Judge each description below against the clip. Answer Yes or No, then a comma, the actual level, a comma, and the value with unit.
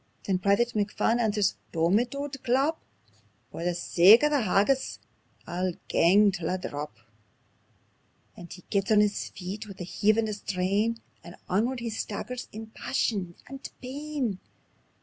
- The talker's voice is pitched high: Yes, high, 210 Hz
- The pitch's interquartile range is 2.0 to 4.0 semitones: No, average, 4.6 semitones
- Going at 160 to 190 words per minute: No, average, 150 wpm